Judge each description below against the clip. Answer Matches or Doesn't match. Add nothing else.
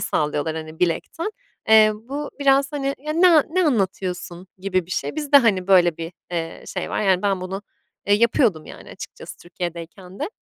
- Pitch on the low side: Doesn't match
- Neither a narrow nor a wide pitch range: Doesn't match